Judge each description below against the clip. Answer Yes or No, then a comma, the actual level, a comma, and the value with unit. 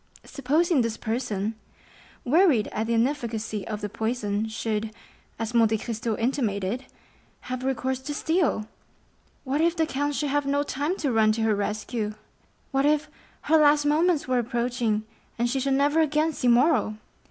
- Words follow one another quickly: No, average, 155 wpm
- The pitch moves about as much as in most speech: Yes, average, 4.7 semitones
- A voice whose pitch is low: No, very high, 250 Hz